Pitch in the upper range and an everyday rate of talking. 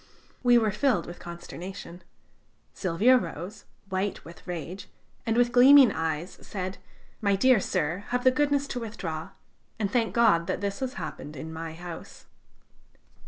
Yes: high, 200 Hz; average, 150 wpm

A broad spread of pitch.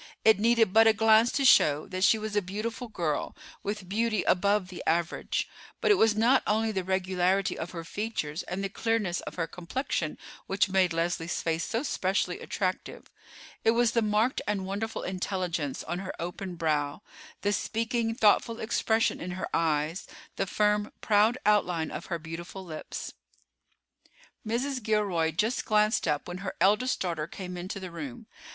No: average, 4.1 semitones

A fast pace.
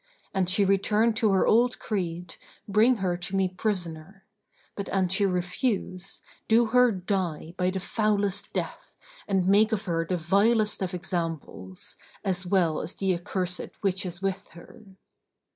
No: average, 155 wpm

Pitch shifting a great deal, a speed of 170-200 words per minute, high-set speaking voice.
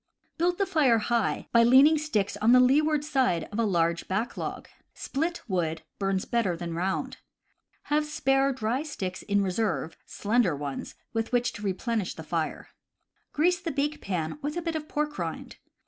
Yes: wide, 7.7 semitones; average, 180 wpm; high, 235 Hz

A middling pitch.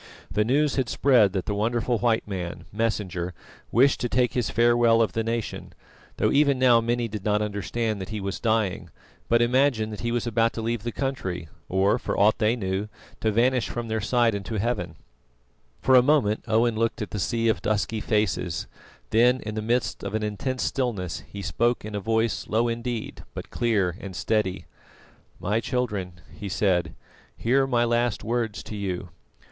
No: low, 110 Hz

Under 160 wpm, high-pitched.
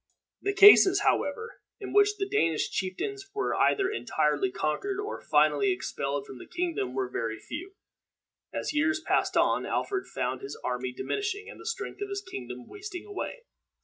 No: average, 165 wpm; very high, 345 Hz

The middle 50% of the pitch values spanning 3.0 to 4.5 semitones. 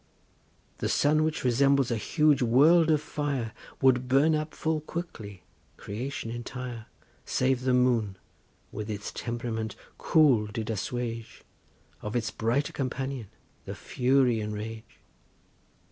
Yes: average, 3.8 semitones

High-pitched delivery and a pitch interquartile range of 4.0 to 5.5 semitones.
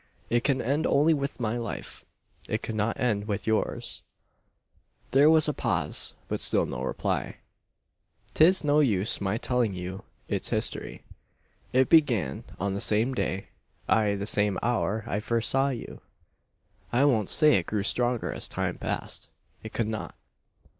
No: low, 115 Hz; average, 4.7 semitones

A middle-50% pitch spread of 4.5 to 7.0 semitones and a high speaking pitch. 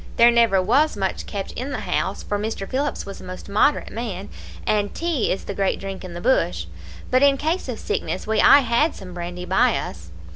Yes: average, 5.3 semitones; high, 210 Hz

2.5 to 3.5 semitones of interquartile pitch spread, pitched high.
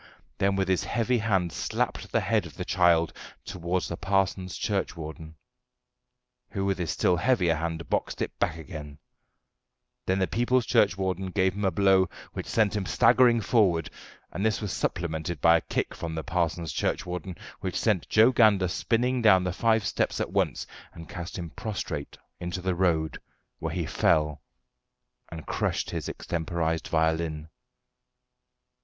No: average, 3.2 semitones; very low, 90 Hz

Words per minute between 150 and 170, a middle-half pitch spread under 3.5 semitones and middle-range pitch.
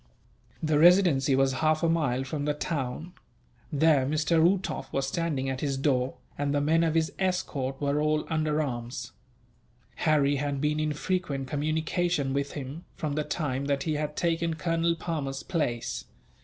Yes: average, 165 wpm; average, 3.0 semitones; medium, 150 Hz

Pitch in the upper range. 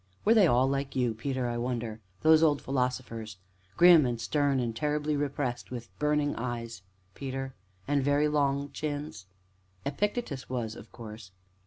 No: low, 135 Hz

